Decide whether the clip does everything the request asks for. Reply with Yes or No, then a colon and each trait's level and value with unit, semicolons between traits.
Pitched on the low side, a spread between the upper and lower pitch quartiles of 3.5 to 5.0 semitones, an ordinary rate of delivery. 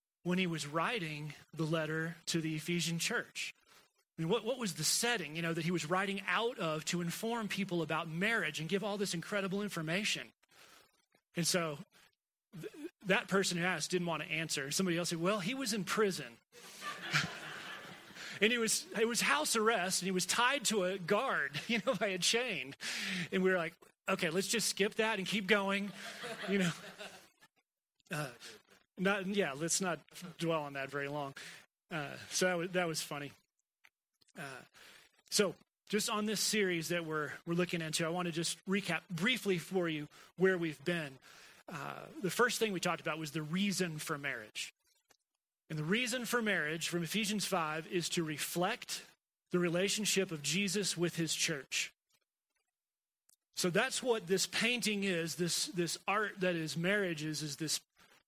No: medium, 180 Hz; average, 3.9 semitones; average, 175 wpm